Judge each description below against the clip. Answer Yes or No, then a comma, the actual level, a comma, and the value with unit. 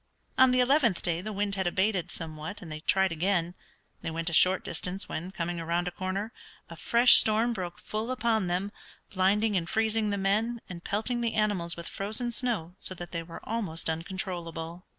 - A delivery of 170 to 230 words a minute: Yes, average, 190 wpm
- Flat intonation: No, average, 4.1 semitones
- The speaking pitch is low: No, high, 190 Hz